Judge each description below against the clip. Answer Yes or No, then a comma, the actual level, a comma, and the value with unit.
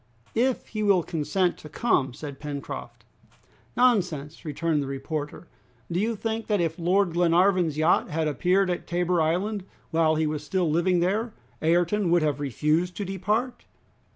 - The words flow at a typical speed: Yes, average, 155 wpm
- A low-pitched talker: No, medium, 175 Hz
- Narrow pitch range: No, average, 3.9 semitones